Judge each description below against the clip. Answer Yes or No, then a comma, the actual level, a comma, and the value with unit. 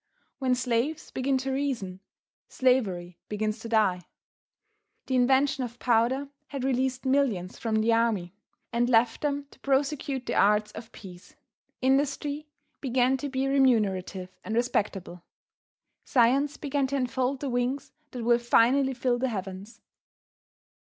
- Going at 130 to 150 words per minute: Yes, slow, 135 wpm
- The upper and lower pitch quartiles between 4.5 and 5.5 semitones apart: No, average, 3.4 semitones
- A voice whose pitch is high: Yes, very high, 250 Hz